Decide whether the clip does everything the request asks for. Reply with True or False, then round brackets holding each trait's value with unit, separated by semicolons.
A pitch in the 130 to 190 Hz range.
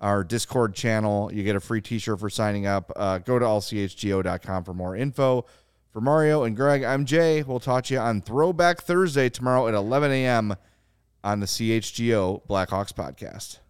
False (115 Hz)